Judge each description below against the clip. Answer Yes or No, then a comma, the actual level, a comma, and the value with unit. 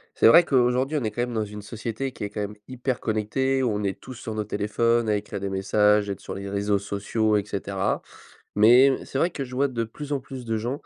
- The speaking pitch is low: Yes, low, 110 Hz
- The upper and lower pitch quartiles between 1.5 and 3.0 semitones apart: No, average, 3.7 semitones